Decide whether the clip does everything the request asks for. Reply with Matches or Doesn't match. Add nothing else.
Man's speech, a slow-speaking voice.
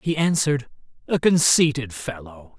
Matches